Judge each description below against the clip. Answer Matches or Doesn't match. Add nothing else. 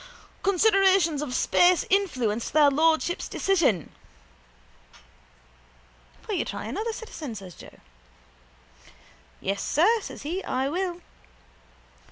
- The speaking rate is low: Matches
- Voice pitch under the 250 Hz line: Doesn't match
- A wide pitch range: Matches